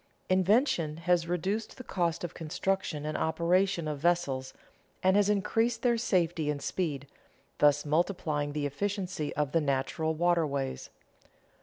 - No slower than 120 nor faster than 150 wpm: Yes, slow, 135 wpm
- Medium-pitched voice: Yes, medium, 170 Hz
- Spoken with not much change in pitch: No, average, 4.1 semitones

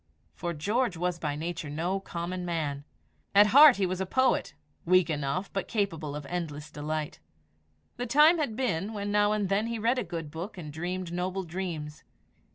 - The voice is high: No, medium, 180 Hz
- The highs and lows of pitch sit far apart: No, average, 4.4 semitones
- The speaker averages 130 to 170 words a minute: No, average, 180 wpm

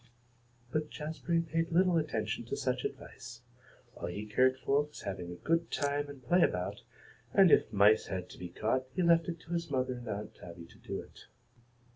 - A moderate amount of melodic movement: No, wide, 7.6 semitones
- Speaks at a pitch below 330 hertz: Yes, medium, 140 Hz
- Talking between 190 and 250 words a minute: Yes, average, 195 wpm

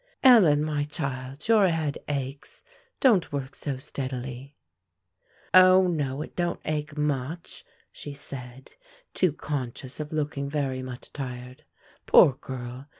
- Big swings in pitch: No, average, 2.9 semitones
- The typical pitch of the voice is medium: Yes, medium, 145 Hz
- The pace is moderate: No, slow, 125 wpm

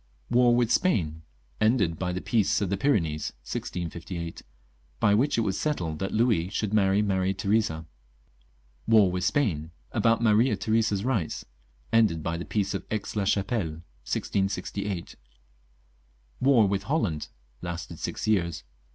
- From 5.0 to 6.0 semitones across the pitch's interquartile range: No, average, 4.5 semitones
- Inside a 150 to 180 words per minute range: No, average, 140 wpm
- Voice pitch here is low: Yes, low, 100 Hz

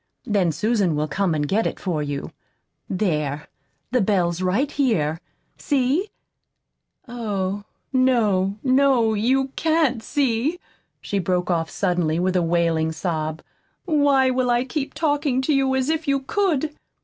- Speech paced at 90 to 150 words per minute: Yes, average, 140 wpm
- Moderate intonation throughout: No, wide, 7.4 semitones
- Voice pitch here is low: No, high, 220 Hz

